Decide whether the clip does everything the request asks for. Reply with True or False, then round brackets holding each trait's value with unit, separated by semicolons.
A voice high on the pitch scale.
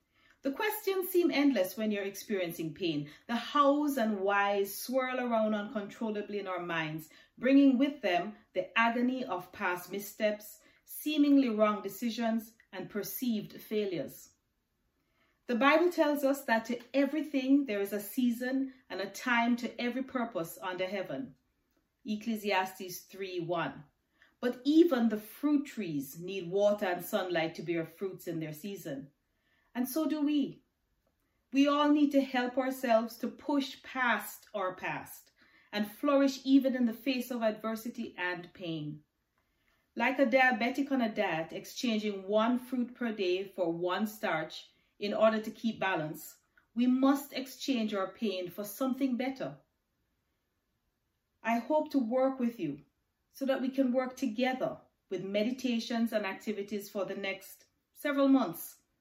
True (230 Hz)